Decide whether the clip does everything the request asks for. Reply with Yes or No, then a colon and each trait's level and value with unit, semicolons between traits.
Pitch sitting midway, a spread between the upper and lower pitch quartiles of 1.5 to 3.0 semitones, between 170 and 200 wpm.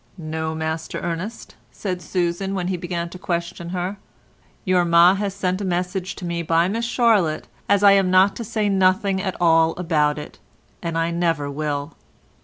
Yes: medium, 175 Hz; narrow, 2.6 semitones; average, 180 wpm